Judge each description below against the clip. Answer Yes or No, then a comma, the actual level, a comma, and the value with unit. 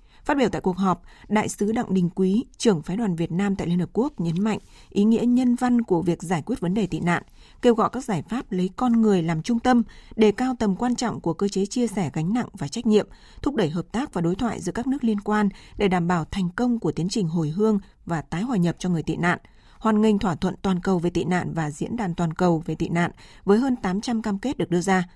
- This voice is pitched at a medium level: No, high, 195 Hz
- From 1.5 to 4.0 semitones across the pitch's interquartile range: No, average, 4.6 semitones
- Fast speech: Yes, fast, 270 wpm